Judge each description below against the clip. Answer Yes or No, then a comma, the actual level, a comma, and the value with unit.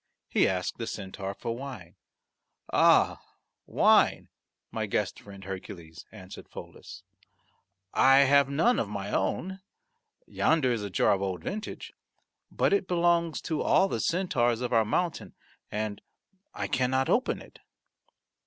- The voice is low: Yes, low, 120 Hz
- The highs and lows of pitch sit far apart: Yes, wide, 8.5 semitones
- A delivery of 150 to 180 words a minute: No, slow, 135 wpm